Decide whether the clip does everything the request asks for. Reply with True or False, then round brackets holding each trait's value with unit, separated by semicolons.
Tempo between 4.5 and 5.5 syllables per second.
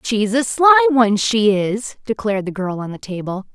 True (4.9 syllables/s)